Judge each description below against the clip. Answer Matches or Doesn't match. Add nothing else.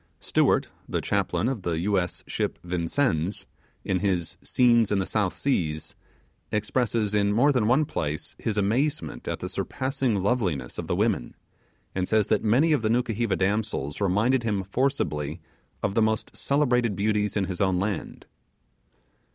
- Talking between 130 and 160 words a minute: Matches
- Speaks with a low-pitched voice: Matches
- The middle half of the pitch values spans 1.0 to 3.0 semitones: Doesn't match